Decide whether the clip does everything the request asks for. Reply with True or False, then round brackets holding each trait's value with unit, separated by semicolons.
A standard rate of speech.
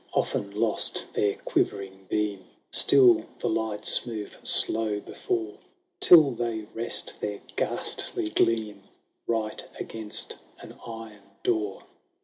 False (110 wpm)